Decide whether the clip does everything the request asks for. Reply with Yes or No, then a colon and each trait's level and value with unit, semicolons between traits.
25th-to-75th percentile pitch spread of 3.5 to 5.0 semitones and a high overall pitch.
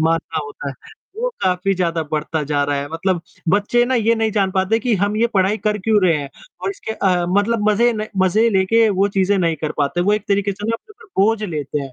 Yes: average, 4.5 semitones; high, 195 Hz